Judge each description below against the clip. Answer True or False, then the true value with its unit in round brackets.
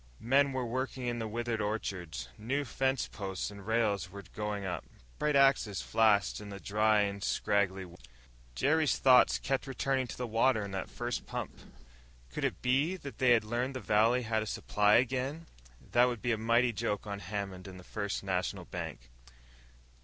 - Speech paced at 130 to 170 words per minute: False (185 wpm)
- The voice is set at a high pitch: False (110 Hz)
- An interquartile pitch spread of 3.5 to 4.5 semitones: True (4.0 semitones)